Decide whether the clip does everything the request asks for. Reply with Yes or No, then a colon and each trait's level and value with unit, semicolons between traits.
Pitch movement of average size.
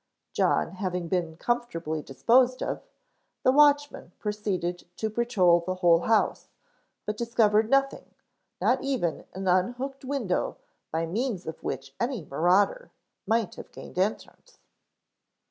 No: wide, 5.8 semitones